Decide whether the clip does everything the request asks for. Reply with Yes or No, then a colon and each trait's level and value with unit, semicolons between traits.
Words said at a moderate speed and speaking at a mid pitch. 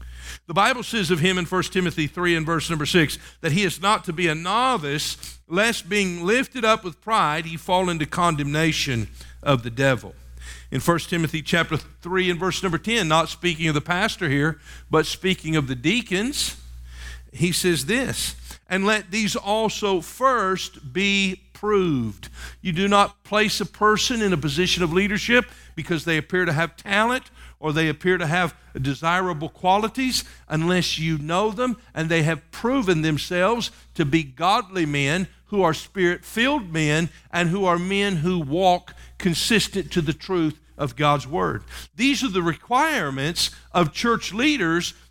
Yes: average, 170 wpm; medium, 175 Hz